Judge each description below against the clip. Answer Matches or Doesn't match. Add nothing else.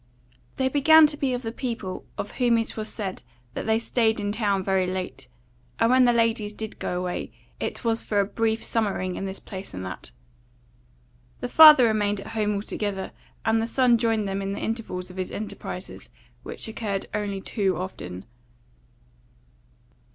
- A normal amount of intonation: Matches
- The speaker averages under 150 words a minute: Doesn't match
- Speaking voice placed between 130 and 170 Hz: Doesn't match